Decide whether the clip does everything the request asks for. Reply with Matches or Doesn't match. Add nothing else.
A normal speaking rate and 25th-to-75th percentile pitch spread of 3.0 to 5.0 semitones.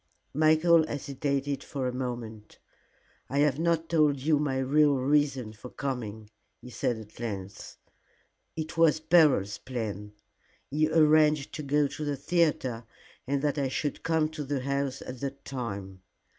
Matches